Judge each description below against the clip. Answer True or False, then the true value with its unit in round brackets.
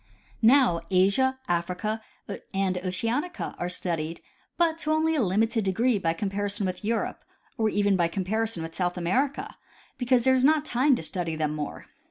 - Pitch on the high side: True (205 Hz)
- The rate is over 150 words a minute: True (170 wpm)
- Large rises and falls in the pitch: True (6.1 semitones)